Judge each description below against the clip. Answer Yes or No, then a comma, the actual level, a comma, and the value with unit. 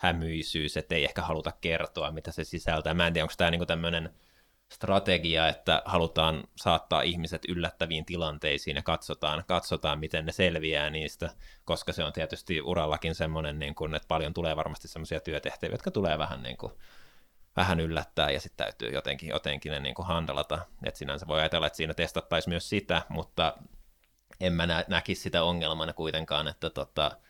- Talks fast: Yes, fast, 170 wpm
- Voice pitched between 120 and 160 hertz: No, very low, 80 Hz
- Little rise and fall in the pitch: Yes, narrow, 1.5 semitones